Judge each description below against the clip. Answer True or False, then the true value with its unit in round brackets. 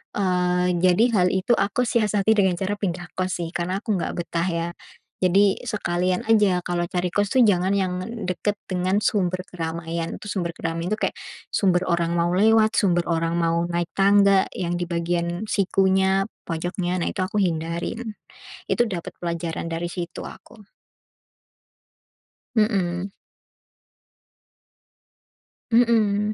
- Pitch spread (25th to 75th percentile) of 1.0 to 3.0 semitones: True (2.7 semitones)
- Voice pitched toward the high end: False (180 Hz)